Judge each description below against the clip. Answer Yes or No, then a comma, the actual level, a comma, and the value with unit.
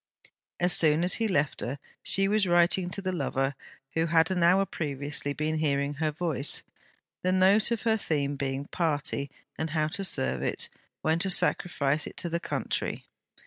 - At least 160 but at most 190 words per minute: Yes, average, 180 wpm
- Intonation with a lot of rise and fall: No, average, 4.2 semitones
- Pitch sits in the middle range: Yes, medium, 160 Hz